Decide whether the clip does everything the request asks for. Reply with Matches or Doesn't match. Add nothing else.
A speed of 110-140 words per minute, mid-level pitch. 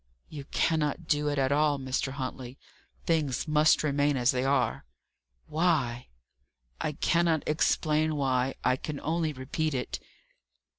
Matches